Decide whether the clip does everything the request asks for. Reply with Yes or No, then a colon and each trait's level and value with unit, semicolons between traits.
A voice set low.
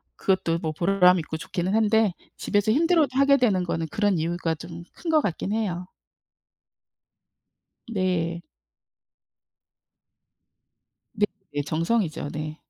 No: medium, 185 Hz